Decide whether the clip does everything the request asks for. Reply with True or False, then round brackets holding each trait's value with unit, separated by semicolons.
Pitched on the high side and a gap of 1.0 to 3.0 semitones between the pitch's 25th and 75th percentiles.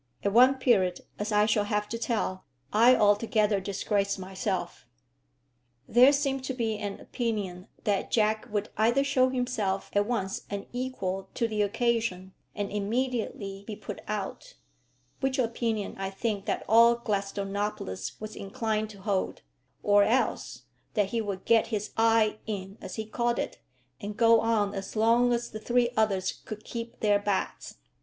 True (215 Hz; 2.7 semitones)